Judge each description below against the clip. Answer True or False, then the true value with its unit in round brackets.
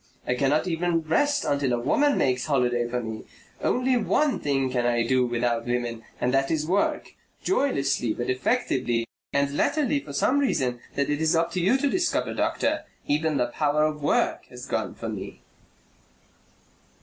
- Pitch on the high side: False (140 Hz)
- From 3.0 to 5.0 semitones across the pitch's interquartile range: False (5.5 semitones)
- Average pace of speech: True (175 wpm)